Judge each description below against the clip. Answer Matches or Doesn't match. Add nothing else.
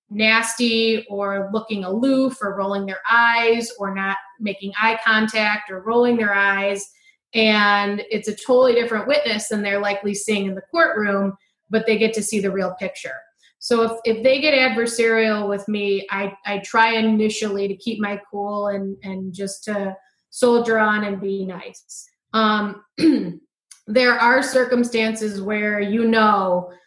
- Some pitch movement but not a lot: Doesn't match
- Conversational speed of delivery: Matches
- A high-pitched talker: Matches